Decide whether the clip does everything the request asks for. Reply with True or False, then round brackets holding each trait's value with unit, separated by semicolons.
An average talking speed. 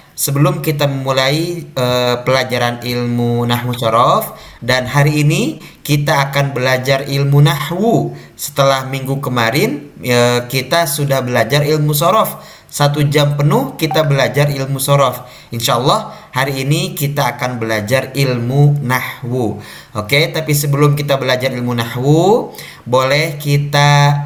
True (125 wpm)